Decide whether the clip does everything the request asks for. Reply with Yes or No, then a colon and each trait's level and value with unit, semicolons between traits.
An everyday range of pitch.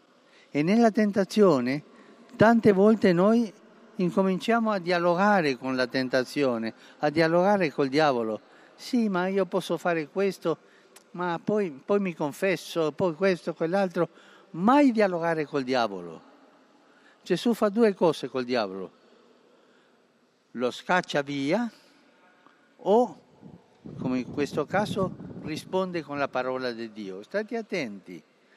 No: wide, 6.7 semitones